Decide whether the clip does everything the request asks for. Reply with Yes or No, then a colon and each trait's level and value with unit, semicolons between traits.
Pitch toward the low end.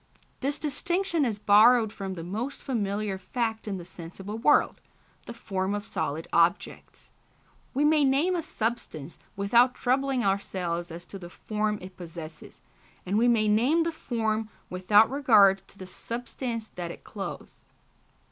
No: high, 215 Hz